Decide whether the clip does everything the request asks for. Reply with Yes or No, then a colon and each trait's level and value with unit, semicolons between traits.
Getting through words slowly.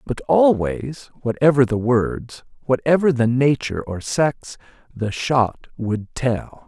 Yes: slow, 125 wpm